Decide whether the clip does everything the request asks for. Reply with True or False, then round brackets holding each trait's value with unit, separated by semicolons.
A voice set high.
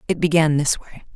False (155 Hz)